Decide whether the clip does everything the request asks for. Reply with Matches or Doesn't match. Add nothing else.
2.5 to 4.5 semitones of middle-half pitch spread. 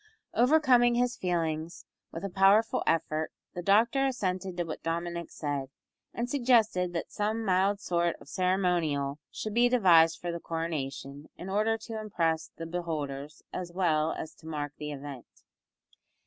Doesn't match